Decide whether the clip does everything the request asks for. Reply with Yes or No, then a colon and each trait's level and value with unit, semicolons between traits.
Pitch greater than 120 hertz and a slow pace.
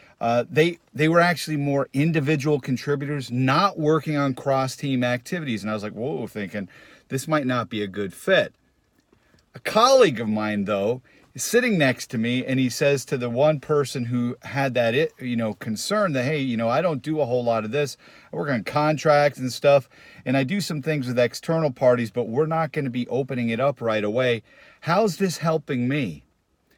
No: low, 135 Hz; fast, 205 wpm